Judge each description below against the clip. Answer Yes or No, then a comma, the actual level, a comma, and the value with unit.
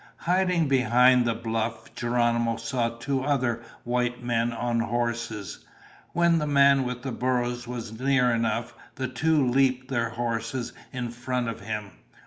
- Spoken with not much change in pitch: Yes, narrow, 1.9 semitones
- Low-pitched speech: Yes, low, 120 Hz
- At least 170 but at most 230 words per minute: No, average, 145 wpm